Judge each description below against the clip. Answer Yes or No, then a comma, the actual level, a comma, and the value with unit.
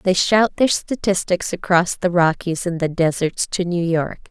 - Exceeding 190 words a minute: No, average, 180 wpm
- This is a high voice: No, medium, 180 Hz